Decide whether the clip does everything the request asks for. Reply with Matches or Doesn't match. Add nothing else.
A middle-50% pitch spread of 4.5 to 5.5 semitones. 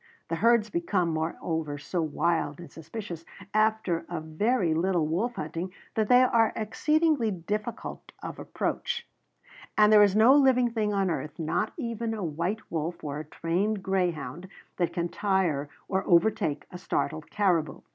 Matches